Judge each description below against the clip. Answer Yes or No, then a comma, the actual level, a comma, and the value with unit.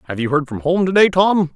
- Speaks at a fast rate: Yes, fast, 310 wpm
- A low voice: No, medium, 165 Hz